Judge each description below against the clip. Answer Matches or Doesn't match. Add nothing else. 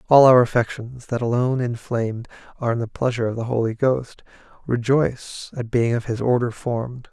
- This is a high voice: Doesn't match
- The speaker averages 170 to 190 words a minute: Matches